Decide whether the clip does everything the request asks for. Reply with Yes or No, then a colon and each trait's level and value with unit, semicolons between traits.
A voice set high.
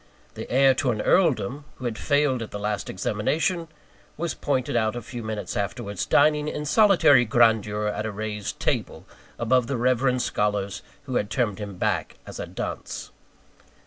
No: low, 120 Hz